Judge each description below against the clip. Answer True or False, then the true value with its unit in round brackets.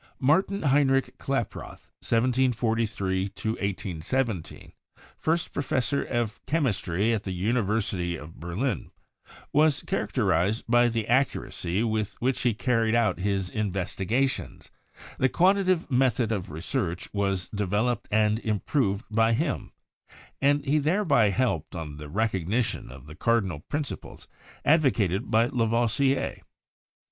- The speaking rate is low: True (120 wpm)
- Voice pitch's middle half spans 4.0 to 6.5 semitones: True (5.2 semitones)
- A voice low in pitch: True (115 Hz)